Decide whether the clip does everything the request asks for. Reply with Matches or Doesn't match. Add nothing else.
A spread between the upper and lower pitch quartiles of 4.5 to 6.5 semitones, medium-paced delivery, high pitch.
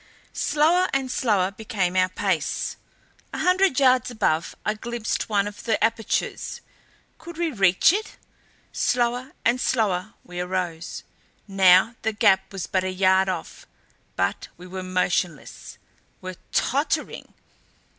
Doesn't match